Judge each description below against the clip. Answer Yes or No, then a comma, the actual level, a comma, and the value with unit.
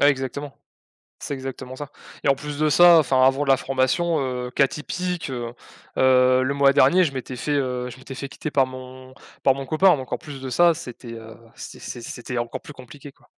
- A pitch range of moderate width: No, narrow, 2.2 semitones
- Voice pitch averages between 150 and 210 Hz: No, low, 135 Hz